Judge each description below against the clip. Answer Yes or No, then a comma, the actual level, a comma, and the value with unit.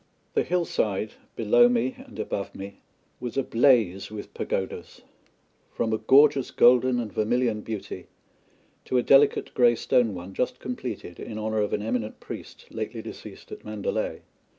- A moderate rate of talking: Yes, average, 150 wpm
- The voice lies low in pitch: Yes, low, 115 Hz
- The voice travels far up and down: No, average, 2.8 semitones